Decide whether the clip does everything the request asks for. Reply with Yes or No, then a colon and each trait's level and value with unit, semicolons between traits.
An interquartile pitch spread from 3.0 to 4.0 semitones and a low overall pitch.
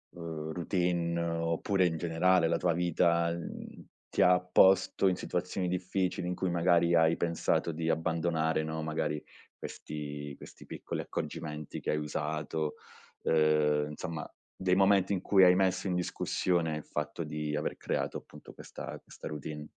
No: narrow, 2.6 semitones; very low, 85 Hz